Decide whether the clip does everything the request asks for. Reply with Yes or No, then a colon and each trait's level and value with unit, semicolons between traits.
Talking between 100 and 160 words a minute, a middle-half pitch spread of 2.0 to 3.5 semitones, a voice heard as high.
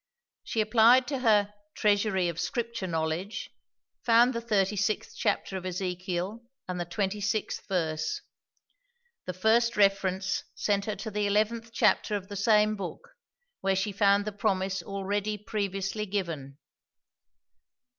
Yes: slow, 135 wpm; narrow, 2.4 semitones; high, 200 Hz